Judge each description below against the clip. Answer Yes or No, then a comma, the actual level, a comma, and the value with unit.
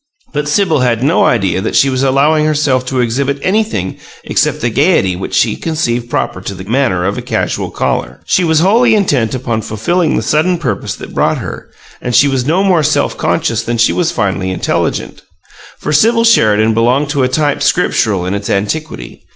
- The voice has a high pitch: No, low, 135 Hz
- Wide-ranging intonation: Yes, wide, 6.1 semitones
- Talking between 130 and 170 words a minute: No, average, 190 wpm